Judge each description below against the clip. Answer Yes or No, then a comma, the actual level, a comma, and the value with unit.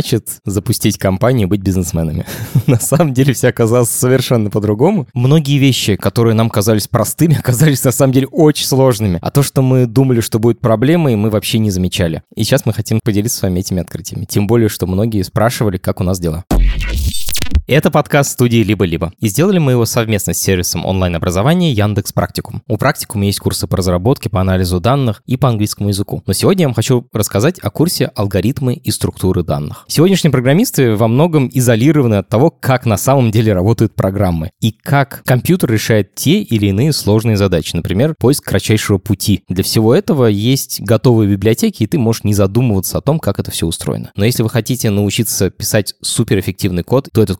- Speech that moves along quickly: Yes, fast, 185 wpm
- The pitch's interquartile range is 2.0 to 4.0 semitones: No, average, 4.5 semitones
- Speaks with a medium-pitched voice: No, low, 110 Hz